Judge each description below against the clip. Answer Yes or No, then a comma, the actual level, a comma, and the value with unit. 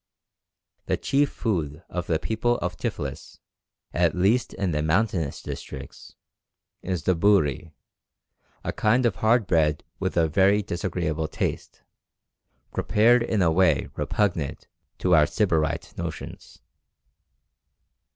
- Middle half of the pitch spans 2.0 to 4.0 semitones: No, average, 4.8 semitones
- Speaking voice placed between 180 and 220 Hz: No, very low, 90 Hz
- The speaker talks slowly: Yes, slow, 120 wpm